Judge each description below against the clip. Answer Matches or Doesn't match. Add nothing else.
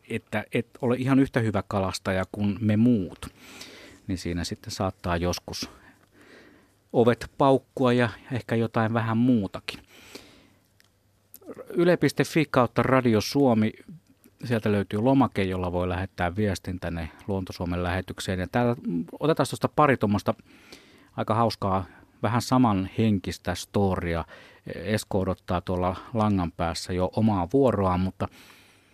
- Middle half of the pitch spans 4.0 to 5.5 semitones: Matches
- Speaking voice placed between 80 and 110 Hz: Matches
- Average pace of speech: Matches